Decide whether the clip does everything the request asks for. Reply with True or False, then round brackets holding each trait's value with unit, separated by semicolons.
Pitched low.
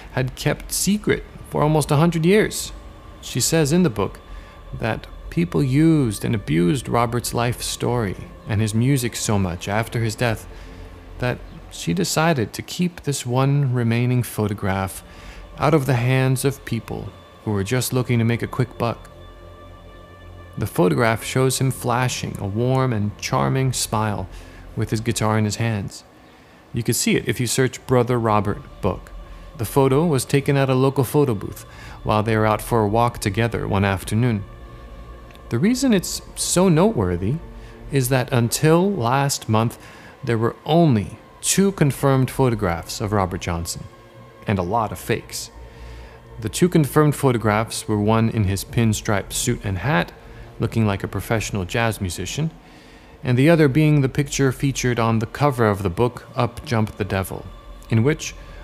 True (115 Hz)